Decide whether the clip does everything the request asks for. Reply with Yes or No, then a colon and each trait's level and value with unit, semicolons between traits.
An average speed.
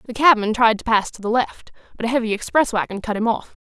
No: fast, 265 wpm